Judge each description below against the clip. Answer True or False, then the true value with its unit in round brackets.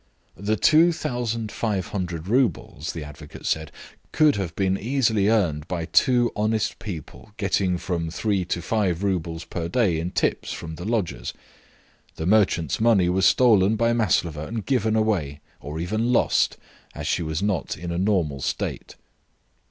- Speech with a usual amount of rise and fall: True (4.8 semitones)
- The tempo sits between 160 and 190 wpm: False (150 wpm)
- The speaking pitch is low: True (95 Hz)